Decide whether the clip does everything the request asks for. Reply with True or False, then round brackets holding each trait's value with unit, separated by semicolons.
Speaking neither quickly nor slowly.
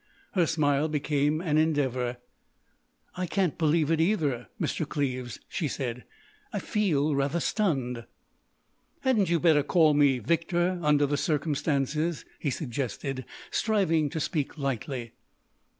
False (120 wpm)